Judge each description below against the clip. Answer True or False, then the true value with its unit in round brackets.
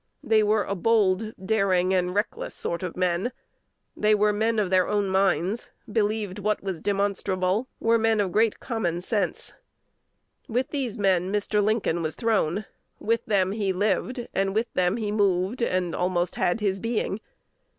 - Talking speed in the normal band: True (160 wpm)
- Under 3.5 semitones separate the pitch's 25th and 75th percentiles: True (2.9 semitones)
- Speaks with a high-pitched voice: True (205 Hz)